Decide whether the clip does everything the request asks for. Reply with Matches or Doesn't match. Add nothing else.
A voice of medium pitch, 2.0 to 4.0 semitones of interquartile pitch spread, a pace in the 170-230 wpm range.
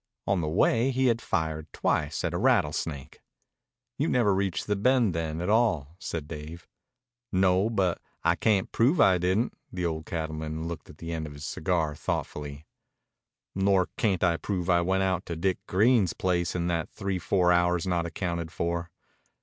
Doesn't match